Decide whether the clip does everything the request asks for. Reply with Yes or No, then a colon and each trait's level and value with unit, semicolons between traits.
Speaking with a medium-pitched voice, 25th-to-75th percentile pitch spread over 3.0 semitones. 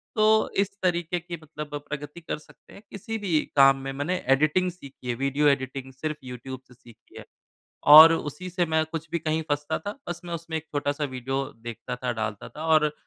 Yes: medium, 150 Hz; average, 3.8 semitones